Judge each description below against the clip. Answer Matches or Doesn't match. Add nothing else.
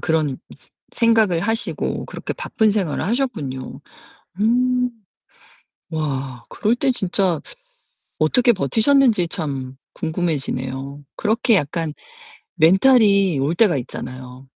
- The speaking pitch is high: Doesn't match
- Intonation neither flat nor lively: Doesn't match